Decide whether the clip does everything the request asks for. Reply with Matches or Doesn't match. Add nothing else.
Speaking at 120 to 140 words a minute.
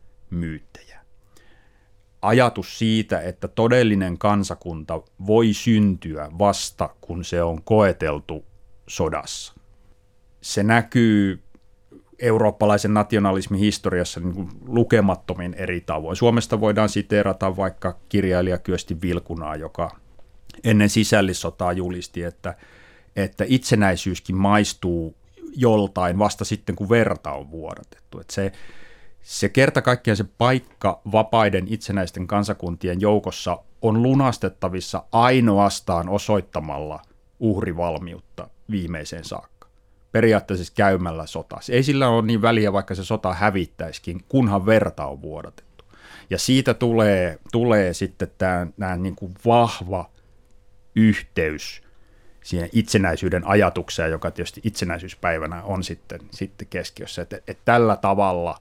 Doesn't match